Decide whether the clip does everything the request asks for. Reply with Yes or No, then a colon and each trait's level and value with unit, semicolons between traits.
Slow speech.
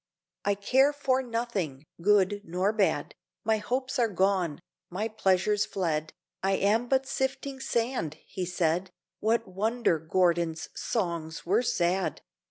Yes: slow, 130 wpm